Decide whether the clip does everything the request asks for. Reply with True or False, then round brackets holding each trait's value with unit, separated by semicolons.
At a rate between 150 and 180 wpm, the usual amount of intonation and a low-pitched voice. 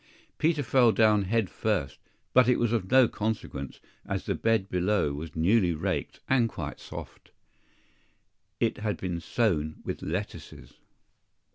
False (140 wpm; 4.7 semitones; 105 Hz)